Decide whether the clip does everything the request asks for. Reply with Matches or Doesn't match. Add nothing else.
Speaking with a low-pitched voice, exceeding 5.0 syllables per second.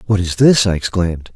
Matches